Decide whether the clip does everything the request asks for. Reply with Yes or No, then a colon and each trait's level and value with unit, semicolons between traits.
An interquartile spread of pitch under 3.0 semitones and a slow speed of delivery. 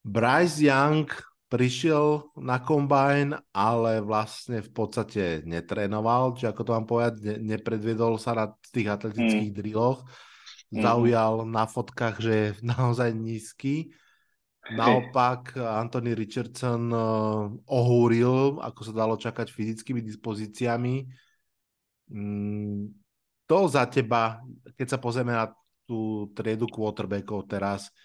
Yes: narrow, 2.4 semitones; slow, 105 wpm